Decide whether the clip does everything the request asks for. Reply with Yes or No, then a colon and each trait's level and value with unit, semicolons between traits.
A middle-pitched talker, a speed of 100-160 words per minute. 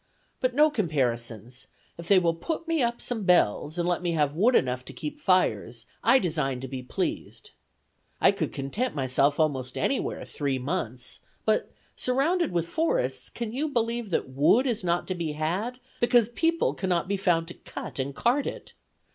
No: medium, 175 Hz; average, 180 wpm